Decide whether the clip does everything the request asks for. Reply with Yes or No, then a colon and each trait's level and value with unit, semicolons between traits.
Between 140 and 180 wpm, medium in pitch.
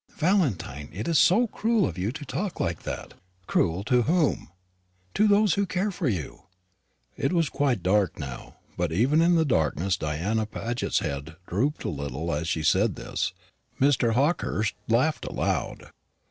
No: average, 160 wpm; low, 115 Hz